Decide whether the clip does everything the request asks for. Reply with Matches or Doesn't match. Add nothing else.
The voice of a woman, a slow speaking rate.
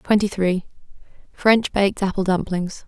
Matches